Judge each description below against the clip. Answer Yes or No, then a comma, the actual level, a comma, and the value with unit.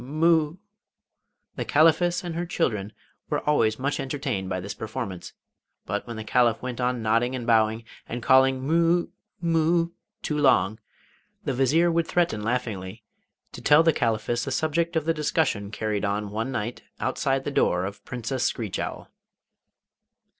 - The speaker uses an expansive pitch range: Yes, wide, 6.4 semitones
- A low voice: Yes, low, 130 Hz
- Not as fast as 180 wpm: Yes, average, 155 wpm